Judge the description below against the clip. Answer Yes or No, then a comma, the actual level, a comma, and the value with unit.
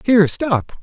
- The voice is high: Yes, high, 205 Hz